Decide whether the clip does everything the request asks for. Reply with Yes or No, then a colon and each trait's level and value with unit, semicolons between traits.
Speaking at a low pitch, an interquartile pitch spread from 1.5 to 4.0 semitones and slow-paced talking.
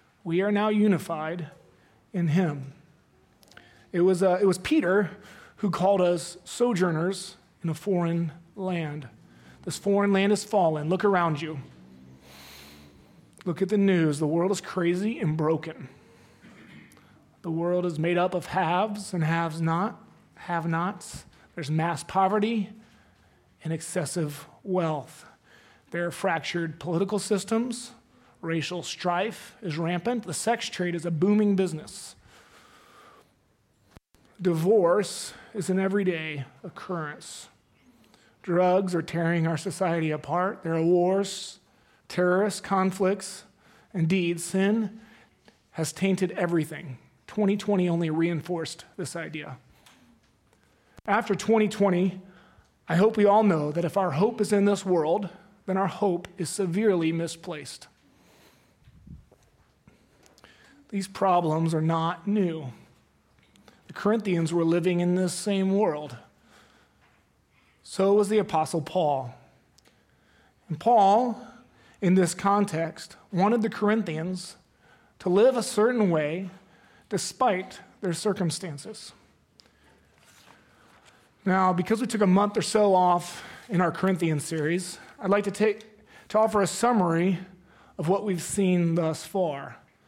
No: medium, 180 Hz; average, 3.5 semitones; slow, 120 wpm